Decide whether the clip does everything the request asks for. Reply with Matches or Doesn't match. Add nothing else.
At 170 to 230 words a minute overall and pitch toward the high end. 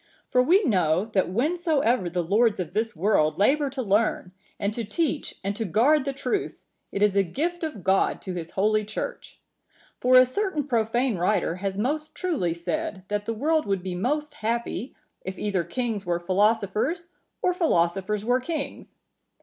Matches